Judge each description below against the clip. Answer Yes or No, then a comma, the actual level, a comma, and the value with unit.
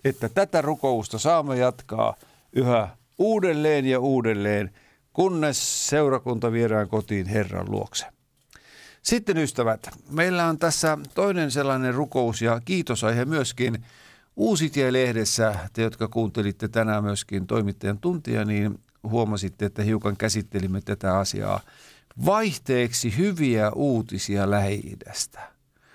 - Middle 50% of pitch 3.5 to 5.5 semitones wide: Yes, average, 5.2 semitones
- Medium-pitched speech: No, low, 115 Hz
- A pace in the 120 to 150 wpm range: No, average, 105 wpm